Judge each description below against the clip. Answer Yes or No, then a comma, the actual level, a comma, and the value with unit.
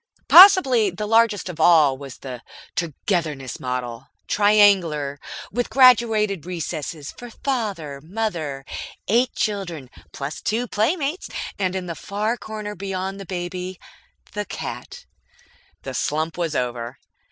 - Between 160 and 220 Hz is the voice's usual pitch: Yes, medium, 185 Hz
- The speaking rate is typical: No, slow, 120 wpm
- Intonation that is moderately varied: No, wide, 6.1 semitones